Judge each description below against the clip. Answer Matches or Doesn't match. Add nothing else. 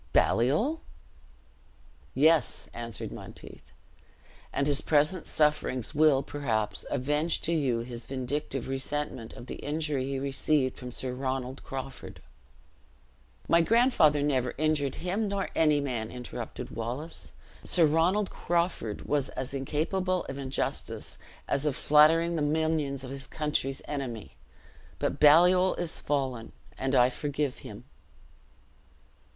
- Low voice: Doesn't match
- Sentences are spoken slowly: Matches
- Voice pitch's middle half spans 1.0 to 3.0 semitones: Doesn't match